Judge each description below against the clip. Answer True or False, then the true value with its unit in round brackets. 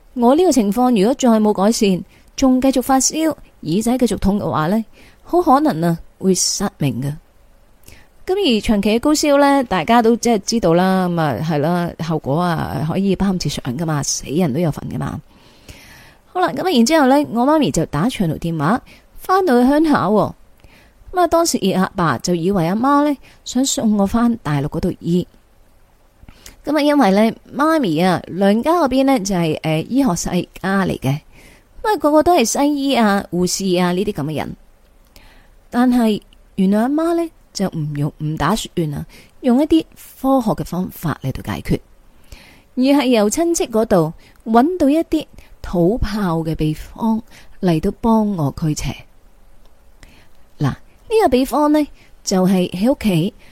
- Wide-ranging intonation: True (8.0 semitones)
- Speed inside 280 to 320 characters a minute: False (240 characters per minute)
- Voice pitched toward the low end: False (210 Hz)